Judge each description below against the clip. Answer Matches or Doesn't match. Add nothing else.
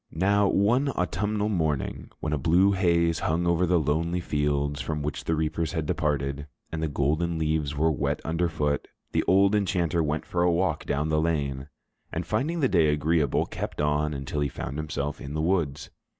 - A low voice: Matches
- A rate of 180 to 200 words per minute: Matches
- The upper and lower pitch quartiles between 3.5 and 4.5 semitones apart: Doesn't match